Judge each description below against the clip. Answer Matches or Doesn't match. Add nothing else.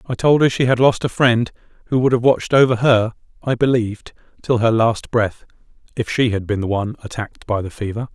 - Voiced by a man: Matches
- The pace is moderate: Doesn't match